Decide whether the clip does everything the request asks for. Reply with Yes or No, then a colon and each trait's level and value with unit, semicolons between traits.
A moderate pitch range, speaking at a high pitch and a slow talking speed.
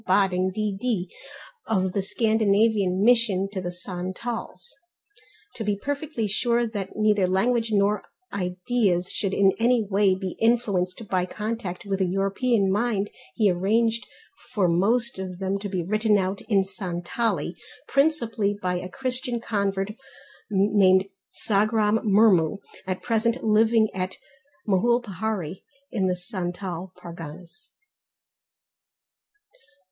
Yes: average, 3.2 semitones; high, 200 Hz; slow, 120 wpm